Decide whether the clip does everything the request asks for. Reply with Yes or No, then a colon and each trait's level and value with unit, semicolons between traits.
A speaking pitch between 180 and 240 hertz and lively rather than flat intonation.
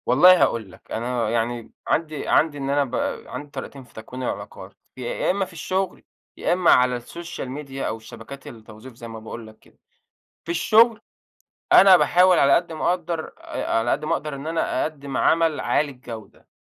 No: medium, 140 Hz; wide, 5.8 semitones